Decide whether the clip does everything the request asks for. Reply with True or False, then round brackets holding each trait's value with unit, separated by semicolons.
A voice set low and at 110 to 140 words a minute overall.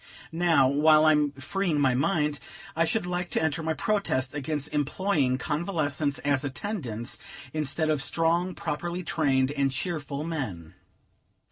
False (150 Hz; 135 wpm)